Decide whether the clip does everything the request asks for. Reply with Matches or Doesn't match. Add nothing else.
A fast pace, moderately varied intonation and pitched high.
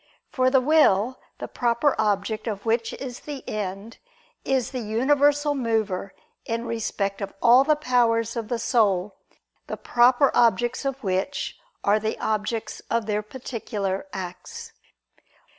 Doesn't match